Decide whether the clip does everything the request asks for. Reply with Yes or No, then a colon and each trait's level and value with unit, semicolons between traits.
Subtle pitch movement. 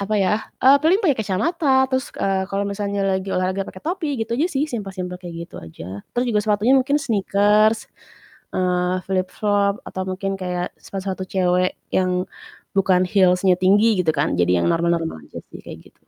No: average, 3.1 semitones